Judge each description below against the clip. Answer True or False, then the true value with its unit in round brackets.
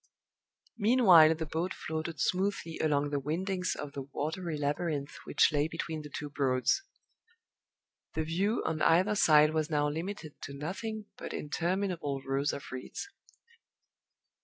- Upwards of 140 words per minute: False (135 wpm)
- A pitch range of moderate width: True (3.8 semitones)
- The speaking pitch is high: False (160 Hz)